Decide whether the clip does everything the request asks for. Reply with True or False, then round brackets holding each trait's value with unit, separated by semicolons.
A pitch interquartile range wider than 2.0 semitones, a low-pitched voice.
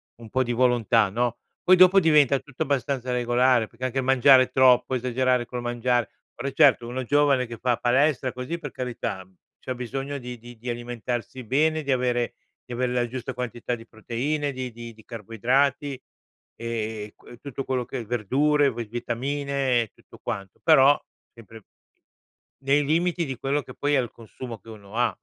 True (2.6 semitones; 125 Hz)